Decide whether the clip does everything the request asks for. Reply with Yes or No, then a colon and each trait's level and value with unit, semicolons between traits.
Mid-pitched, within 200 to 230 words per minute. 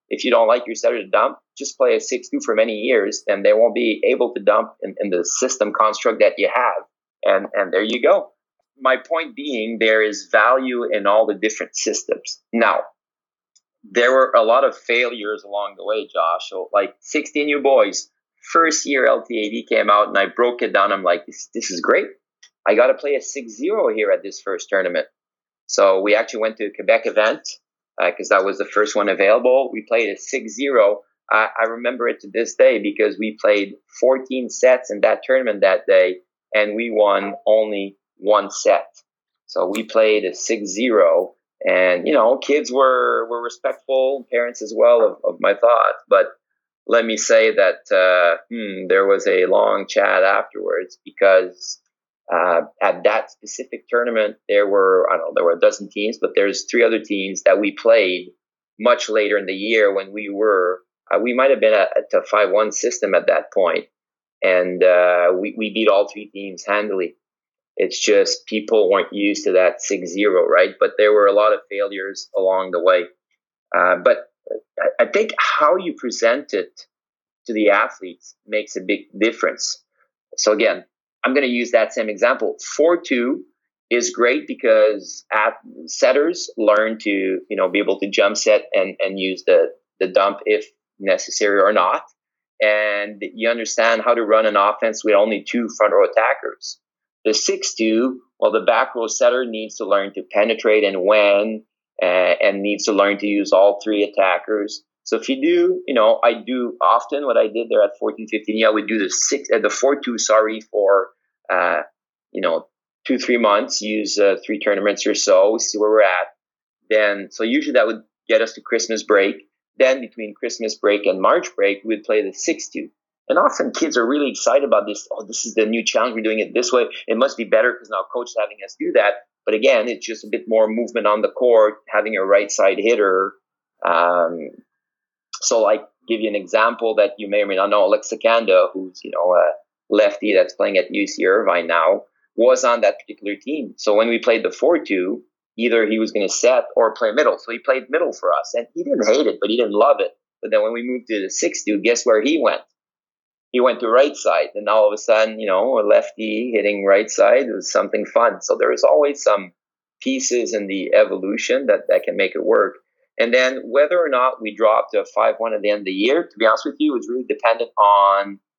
No: low, 130 Hz; fast, 205 wpm